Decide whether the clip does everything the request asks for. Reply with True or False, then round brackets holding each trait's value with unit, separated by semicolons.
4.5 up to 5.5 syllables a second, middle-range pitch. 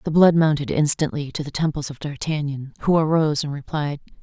False (5.8 syllables/s; 150 Hz)